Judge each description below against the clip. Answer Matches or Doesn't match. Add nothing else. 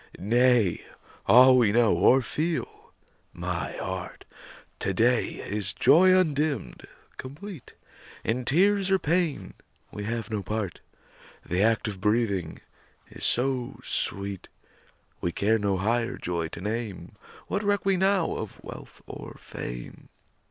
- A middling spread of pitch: Doesn't match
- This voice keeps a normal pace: Doesn't match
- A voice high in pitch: Doesn't match